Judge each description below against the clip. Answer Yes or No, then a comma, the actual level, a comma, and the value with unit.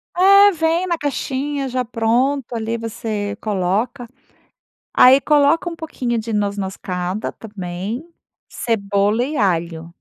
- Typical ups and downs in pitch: No, wide, 5.8 semitones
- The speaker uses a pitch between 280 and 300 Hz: No, high, 230 Hz